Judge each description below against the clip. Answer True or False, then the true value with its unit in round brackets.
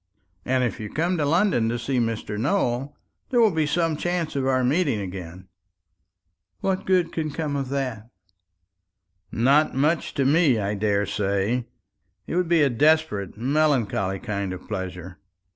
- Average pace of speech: True (155 wpm)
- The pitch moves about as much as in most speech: False (6.8 semitones)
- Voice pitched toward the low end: True (130 Hz)